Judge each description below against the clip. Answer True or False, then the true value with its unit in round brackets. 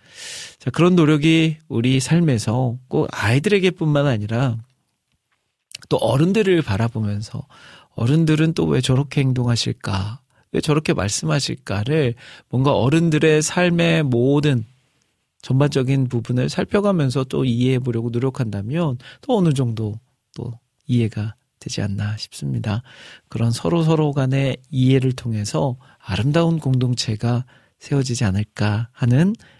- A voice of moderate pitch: False (130 Hz)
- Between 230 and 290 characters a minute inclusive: True (280 characters per minute)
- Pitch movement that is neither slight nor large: True (4.6 semitones)